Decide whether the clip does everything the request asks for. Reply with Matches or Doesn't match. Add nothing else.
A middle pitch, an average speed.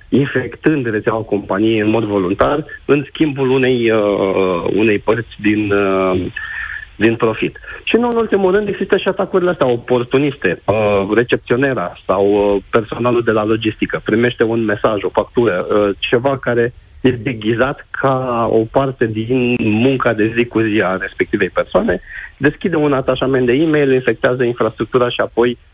Doesn't match